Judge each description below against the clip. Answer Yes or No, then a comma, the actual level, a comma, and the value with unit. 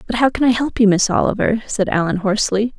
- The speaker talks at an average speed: No, fast, 235 wpm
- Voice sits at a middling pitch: No, high, 215 Hz